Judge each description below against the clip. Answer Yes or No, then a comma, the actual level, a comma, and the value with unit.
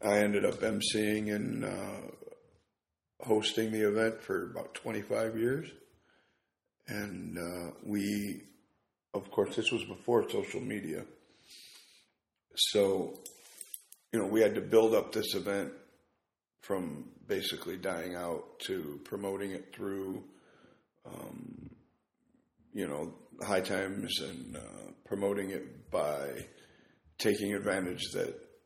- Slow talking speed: Yes, slow, 115 wpm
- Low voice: Yes, low, 105 Hz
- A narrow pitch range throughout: Yes, narrow, 2.2 semitones